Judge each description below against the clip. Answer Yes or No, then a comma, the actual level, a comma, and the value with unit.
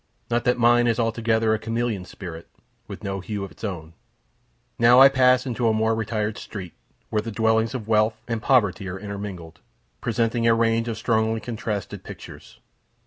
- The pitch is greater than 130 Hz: No, low, 110 Hz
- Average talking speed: Yes, average, 175 wpm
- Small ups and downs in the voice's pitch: Yes, narrow, 2.2 semitones